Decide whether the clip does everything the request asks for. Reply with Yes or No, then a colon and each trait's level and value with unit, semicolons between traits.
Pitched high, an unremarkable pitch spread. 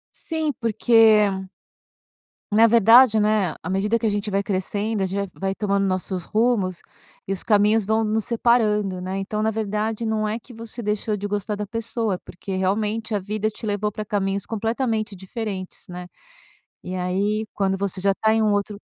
No: high, 210 Hz; narrow, 2.2 semitones